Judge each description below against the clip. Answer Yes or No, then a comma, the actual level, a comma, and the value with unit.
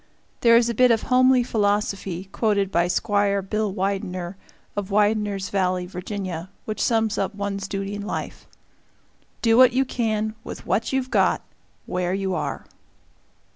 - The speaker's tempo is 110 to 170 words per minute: Yes, average, 150 wpm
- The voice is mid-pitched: No, high, 205 Hz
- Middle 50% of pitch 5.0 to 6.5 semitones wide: No, average, 2.7 semitones